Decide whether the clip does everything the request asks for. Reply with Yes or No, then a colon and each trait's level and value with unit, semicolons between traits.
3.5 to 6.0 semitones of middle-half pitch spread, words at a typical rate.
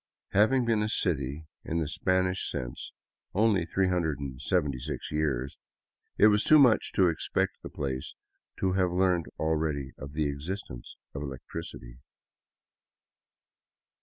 No: wide, 5.4 semitones; slow, 120 wpm